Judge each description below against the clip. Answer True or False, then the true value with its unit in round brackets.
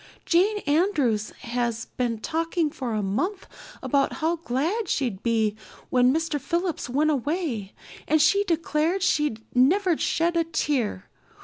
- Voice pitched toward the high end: True (300 Hz)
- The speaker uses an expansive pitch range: True (5.8 semitones)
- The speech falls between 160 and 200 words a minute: False (135 wpm)